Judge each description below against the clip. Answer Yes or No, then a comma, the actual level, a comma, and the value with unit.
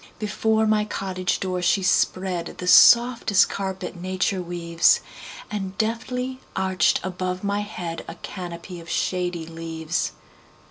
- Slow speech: Yes, slow, 105 wpm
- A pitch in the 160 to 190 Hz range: Yes, medium, 185 Hz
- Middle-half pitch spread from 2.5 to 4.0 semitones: Yes, average, 2.9 semitones